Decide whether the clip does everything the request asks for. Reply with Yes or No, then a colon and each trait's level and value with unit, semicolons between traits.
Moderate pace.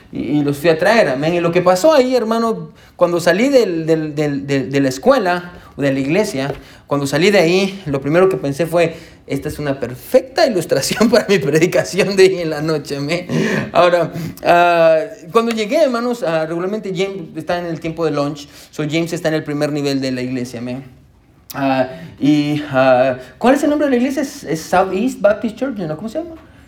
No: fast, 210 wpm